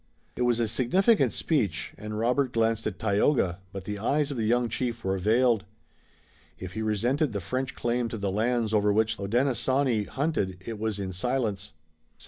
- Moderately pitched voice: No, low, 115 Hz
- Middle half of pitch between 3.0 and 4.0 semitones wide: Yes, average, 3.3 semitones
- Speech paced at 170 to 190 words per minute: Yes, average, 185 wpm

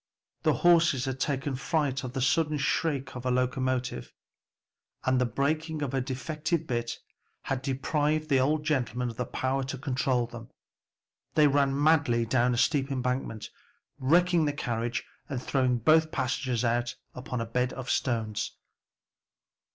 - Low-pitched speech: Yes, low, 130 Hz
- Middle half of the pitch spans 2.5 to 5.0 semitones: Yes, average, 3.0 semitones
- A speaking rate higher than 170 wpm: No, average, 150 wpm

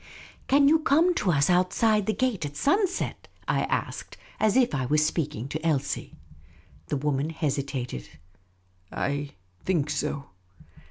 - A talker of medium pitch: Yes, medium, 155 Hz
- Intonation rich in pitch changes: Yes, wide, 7.5 semitones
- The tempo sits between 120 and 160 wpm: Yes, average, 145 wpm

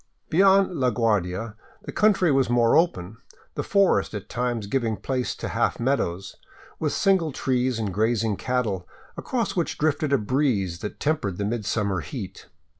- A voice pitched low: Yes, low, 120 Hz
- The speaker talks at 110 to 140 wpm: No, average, 155 wpm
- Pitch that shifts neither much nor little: No, wide, 6.4 semitones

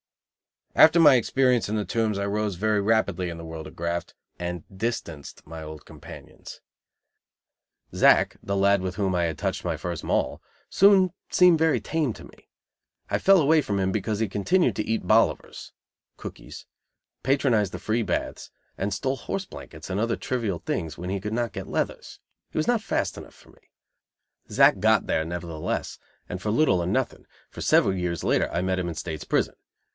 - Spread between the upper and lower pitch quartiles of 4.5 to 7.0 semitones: Yes, wide, 5.5 semitones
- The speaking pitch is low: Yes, low, 100 Hz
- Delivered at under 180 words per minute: No, average, 185 wpm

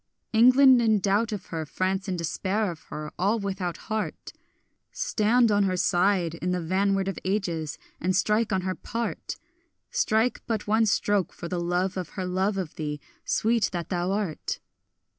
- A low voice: No, high, 195 Hz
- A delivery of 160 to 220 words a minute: Yes, average, 170 wpm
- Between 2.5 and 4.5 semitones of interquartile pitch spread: Yes, average, 3.1 semitones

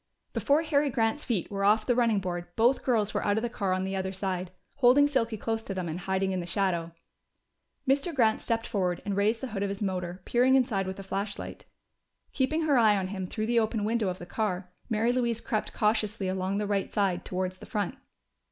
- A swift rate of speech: Yes, fast, 225 wpm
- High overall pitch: Yes, high, 205 Hz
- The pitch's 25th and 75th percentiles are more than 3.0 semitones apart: Yes, average, 3.7 semitones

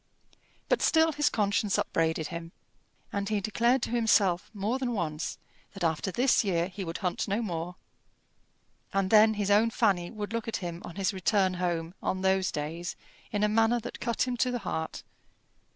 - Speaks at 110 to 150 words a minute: No, average, 185 wpm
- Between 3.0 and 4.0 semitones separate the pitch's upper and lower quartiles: No, average, 4.4 semitones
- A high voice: Yes, high, 200 Hz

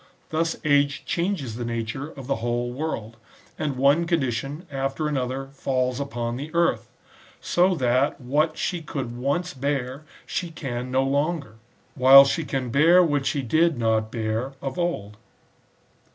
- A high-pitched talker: No, low, 135 Hz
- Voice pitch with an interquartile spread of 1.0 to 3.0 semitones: No, average, 3.9 semitones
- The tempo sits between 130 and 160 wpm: Yes, average, 155 wpm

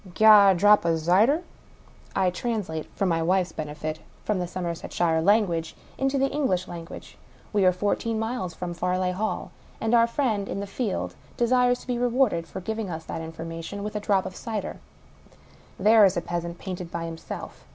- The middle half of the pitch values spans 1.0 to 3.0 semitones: No, average, 4.4 semitones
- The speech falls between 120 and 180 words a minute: No, average, 190 wpm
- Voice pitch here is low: No, high, 190 Hz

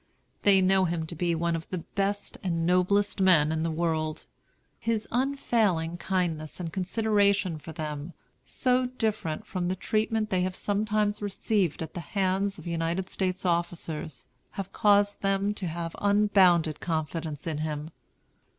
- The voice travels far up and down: No, average, 3.7 semitones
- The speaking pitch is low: No, medium, 185 Hz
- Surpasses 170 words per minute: No, average, 150 wpm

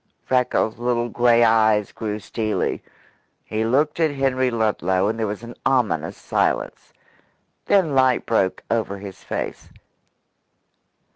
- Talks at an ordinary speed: No, slow, 125 wpm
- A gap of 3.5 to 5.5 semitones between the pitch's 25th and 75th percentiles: No, average, 3.0 semitones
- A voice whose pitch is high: No, low, 115 Hz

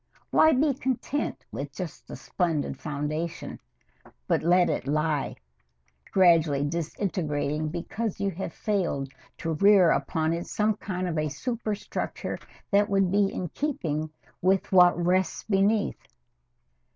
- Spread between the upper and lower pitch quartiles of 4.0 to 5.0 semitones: Yes, average, 4.4 semitones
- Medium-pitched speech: Yes, medium, 180 Hz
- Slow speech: Yes, slow, 125 wpm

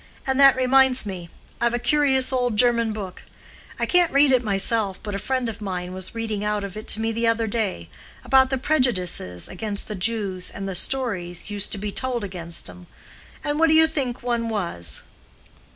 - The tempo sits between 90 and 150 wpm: No, average, 190 wpm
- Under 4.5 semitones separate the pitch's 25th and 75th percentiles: No, average, 4.9 semitones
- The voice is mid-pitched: No, high, 225 Hz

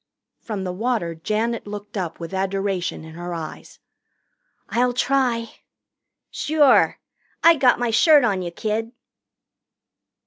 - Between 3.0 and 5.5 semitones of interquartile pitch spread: Yes, average, 5.0 semitones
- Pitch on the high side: Yes, high, 215 Hz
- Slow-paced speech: Yes, slow, 125 wpm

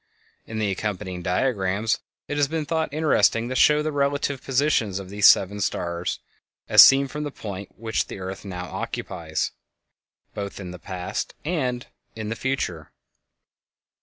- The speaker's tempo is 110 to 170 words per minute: Yes, average, 155 wpm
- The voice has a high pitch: No, low, 110 Hz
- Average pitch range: No, wide, 6.8 semitones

